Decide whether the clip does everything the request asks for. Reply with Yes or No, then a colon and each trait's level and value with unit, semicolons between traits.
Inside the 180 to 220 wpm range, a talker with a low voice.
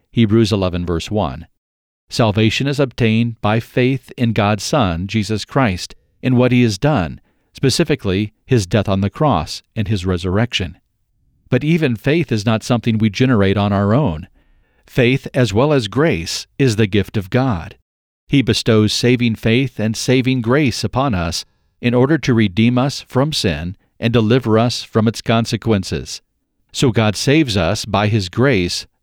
No: average, 160 wpm; low, 115 Hz